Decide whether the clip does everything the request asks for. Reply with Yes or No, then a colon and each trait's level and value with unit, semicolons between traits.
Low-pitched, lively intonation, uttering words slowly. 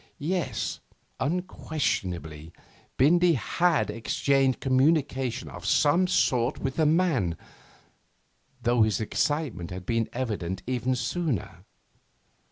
Yes: low, 130 Hz; wide, 6.2 semitones; slow, 95 wpm